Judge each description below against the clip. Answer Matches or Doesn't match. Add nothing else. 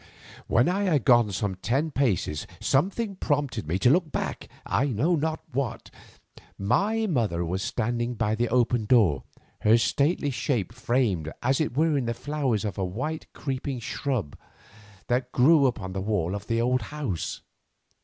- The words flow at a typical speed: Matches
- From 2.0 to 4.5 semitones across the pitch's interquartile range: Doesn't match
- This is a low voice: Matches